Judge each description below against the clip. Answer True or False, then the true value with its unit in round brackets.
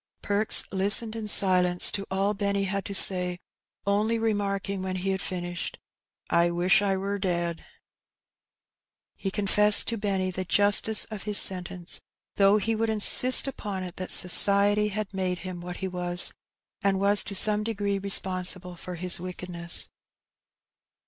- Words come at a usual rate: True (155 wpm)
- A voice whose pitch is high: True (195 Hz)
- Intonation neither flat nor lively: False (2.1 semitones)